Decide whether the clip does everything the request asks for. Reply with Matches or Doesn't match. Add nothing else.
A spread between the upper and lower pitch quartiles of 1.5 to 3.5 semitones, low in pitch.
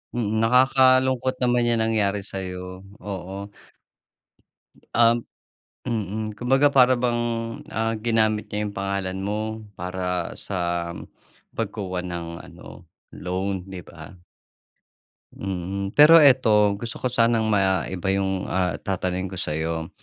Doesn't match